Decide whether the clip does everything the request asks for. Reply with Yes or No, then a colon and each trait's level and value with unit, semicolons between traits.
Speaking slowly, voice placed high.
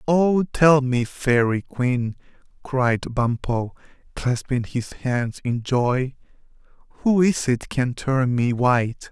No: slow, 125 wpm; low, 130 Hz